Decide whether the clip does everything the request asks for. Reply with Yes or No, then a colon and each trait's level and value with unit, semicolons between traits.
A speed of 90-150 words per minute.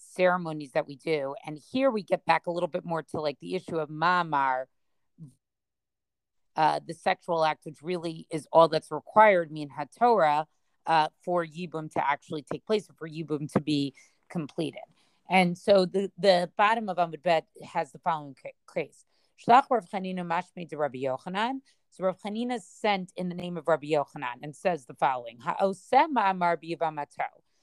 No: average, 165 wpm